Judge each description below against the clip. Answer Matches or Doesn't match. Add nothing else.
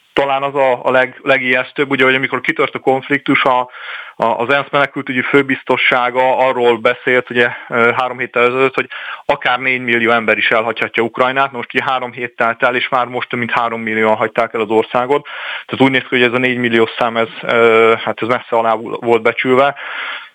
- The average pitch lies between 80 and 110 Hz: Doesn't match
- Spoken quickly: Matches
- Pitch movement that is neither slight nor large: Doesn't match